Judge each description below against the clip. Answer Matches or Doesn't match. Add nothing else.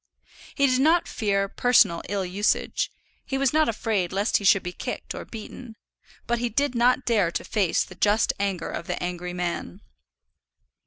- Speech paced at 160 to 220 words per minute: Matches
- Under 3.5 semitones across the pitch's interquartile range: Doesn't match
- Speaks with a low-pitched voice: Doesn't match